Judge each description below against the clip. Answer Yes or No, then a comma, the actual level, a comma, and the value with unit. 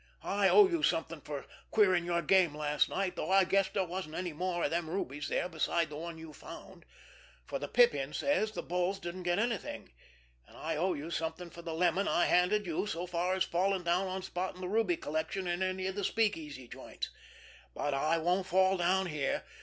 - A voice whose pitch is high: No, medium, 180 Hz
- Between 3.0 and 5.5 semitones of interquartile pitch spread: No, narrow, 2.6 semitones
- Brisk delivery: Yes, fast, 210 wpm